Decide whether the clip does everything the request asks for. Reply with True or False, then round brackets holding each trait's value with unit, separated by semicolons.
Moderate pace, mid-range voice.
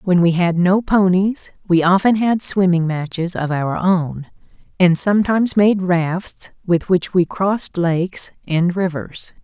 True (155 wpm; 180 Hz)